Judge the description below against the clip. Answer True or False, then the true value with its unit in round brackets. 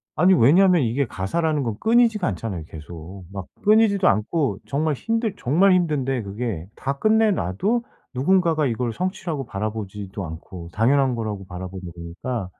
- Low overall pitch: True (125 Hz)